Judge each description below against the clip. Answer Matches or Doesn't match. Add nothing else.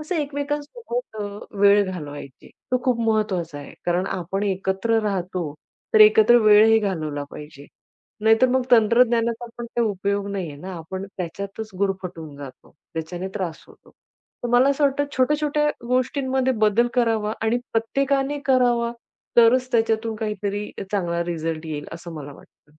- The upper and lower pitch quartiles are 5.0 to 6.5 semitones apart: Matches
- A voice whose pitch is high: Matches